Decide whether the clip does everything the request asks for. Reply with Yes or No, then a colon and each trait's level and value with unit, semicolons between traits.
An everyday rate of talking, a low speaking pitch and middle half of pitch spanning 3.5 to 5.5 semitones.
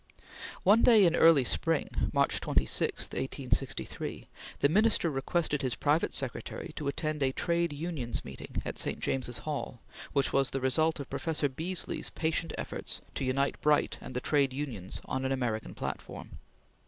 No: average, 155 wpm; medium, 145 Hz; average, 3.8 semitones